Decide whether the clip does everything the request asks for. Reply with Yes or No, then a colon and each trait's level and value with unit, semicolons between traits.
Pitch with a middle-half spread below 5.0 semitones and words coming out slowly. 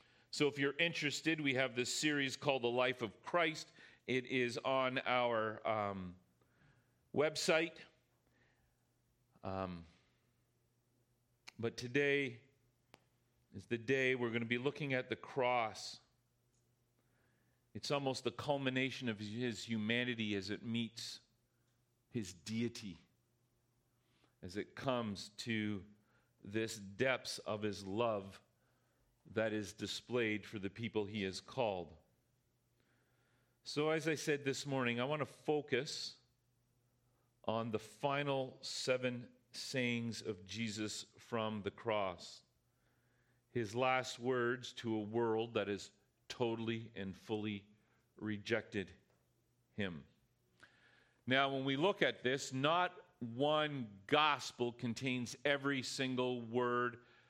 Yes: average, 2.8 semitones; slow, 115 wpm